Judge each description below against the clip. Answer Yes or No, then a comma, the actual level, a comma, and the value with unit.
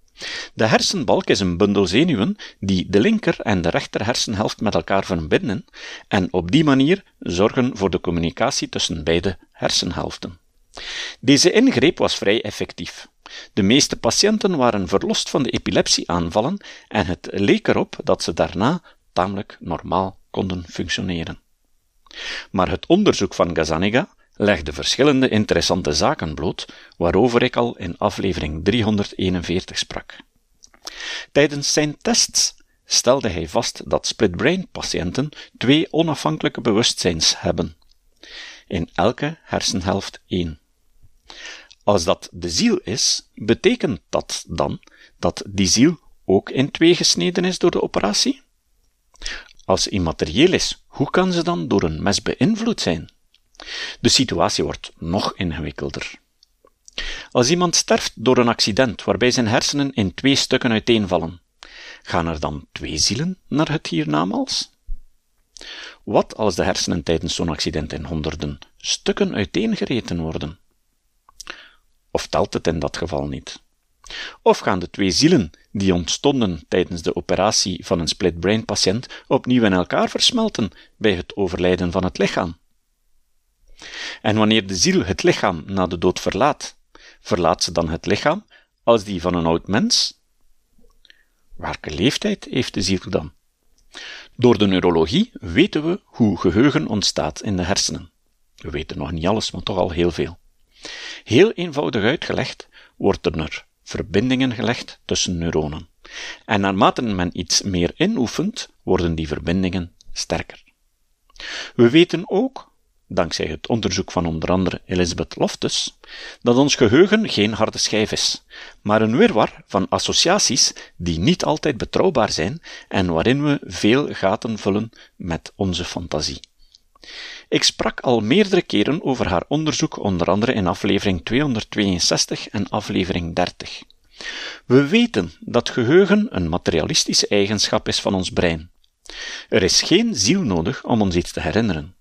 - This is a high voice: No, low, 100 Hz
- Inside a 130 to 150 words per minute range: Yes, average, 140 wpm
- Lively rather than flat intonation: Yes, wide, 6.9 semitones